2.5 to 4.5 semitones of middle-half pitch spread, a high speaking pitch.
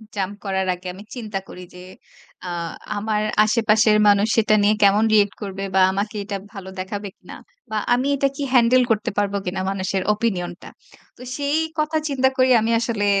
Yes: average, 3.0 semitones; high, 210 Hz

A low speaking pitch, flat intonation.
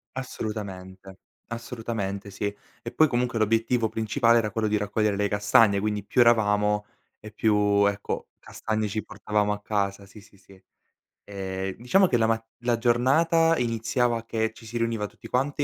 Yes: low, 110 Hz; narrow, 2.3 semitones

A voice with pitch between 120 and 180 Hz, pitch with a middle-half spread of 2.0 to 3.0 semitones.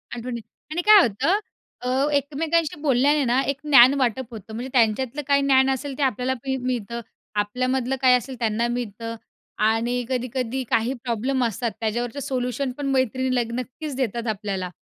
No: very high, 255 Hz; narrow, 2.4 semitones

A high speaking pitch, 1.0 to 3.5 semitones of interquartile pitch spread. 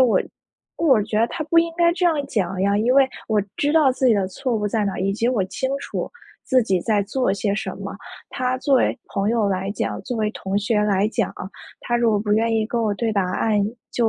No: high, 225 Hz; average, 3.9 semitones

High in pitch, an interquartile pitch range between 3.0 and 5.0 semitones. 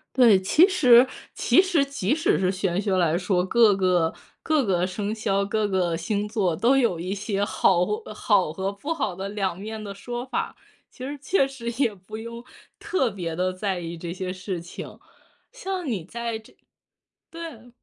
Yes: high, 205 Hz; average, 4.6 semitones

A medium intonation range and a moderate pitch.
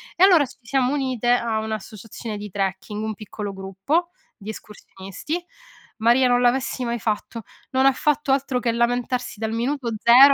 No: average, 3.5 semitones; high, 235 Hz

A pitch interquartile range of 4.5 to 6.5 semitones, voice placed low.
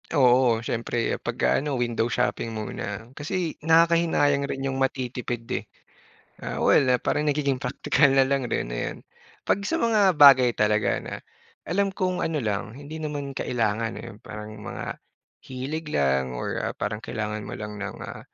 Yes: average, 4.9 semitones; low, 130 Hz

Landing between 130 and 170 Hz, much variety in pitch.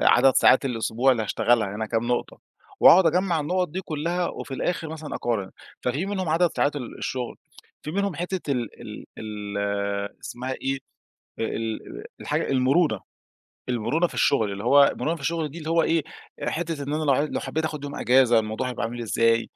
Yes: medium, 140 Hz; wide, 5.7 semitones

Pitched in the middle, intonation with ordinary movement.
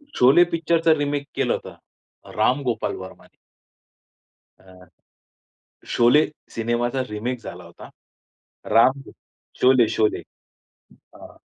No: low, 125 Hz; average, 4.3 semitones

